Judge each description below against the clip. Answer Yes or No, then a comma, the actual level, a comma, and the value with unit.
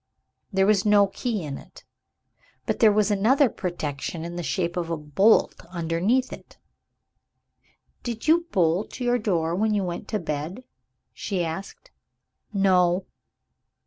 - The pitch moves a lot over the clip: No, average, 4.1 semitones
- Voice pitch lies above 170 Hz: Yes, high, 190 Hz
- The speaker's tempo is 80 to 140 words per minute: Yes, slow, 135 wpm